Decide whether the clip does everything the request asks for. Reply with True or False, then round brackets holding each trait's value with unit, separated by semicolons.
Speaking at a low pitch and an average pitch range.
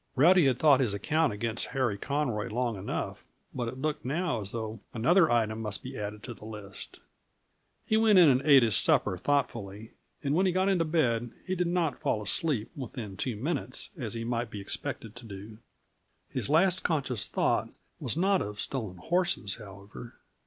False (125 Hz; 6.4 semitones)